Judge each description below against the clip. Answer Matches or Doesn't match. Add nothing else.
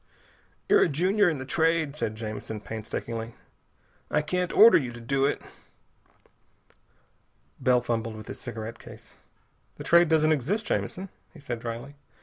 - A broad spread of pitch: Matches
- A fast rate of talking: Doesn't match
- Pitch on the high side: Doesn't match